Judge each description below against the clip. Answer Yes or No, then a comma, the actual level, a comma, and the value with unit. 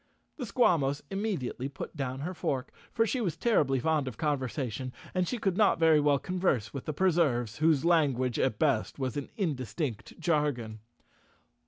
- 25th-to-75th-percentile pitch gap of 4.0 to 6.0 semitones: Yes, average, 5.2 semitones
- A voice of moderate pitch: Yes, medium, 145 Hz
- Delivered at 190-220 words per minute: No, average, 165 wpm